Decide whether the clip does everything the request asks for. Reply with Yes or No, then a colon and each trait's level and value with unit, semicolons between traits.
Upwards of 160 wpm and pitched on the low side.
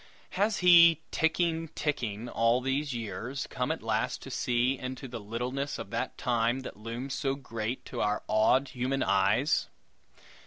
No: average, 155 wpm; low, 130 Hz